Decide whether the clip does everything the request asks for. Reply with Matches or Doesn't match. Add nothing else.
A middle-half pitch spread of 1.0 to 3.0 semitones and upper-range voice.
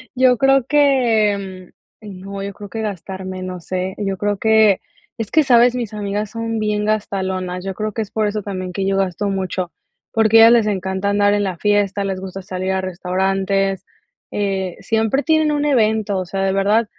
Matches